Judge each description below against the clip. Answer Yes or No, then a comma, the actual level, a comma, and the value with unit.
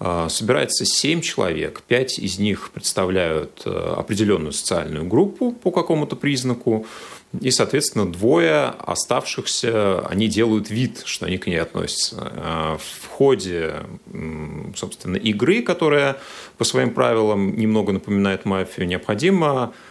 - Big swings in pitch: Yes, wide, 6.1 semitones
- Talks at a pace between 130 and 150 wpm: No, slow, 110 wpm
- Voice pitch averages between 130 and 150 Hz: No, low, 110 Hz